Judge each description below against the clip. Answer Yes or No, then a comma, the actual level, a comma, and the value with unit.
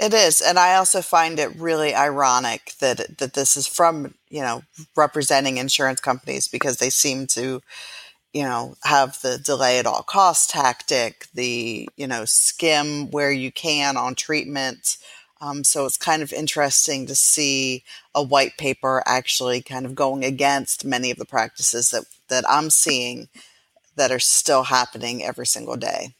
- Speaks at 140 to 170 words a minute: Yes, average, 165 wpm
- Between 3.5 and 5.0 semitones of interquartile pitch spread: No, narrow, 2.4 semitones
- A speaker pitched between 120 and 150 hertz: Yes, low, 135 Hz